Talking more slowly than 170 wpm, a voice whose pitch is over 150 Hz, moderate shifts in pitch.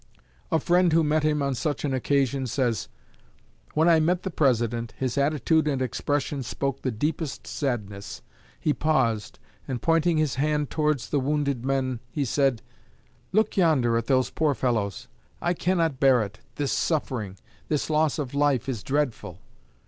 No: average, 160 wpm; medium, 140 Hz; average, 3.7 semitones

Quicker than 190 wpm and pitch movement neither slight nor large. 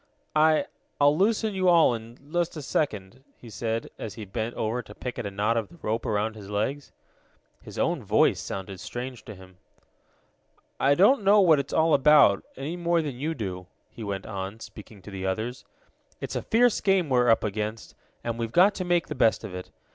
No: fast, 205 wpm; wide, 7.0 semitones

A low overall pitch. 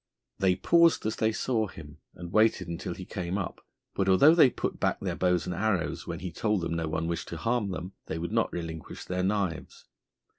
Yes: very low, 95 Hz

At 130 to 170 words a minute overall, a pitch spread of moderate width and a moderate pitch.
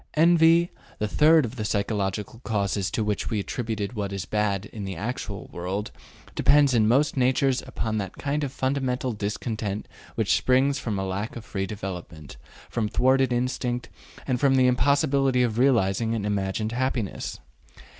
No: average, 160 wpm; average, 4.3 semitones; low, 115 Hz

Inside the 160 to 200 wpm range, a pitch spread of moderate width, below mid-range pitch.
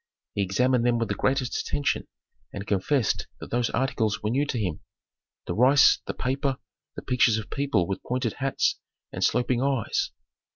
Yes: average, 170 wpm; average, 3.7 semitones; low, 125 Hz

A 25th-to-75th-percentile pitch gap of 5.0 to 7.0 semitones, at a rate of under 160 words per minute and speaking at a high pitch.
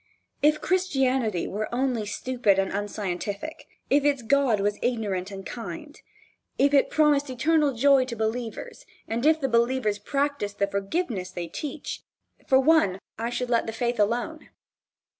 Yes: average, 5.3 semitones; average, 150 wpm; high, 245 Hz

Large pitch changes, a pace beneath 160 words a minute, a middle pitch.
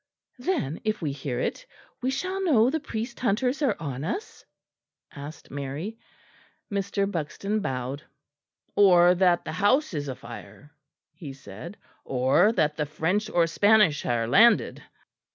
Yes: wide, 7.5 semitones; slow, 135 wpm; medium, 180 Hz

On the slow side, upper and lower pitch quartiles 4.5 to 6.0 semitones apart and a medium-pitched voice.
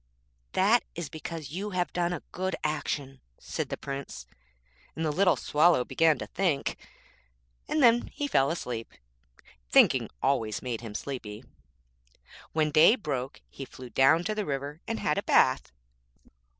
No: average, 150 wpm; average, 4.9 semitones; medium, 155 Hz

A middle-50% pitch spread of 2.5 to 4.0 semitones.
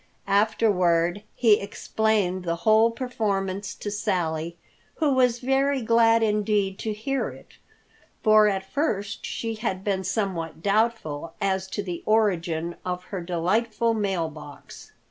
Yes: average, 3.6 semitones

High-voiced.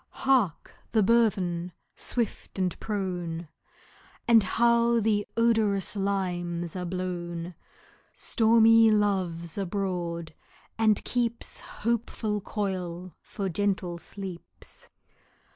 Yes: high, 195 Hz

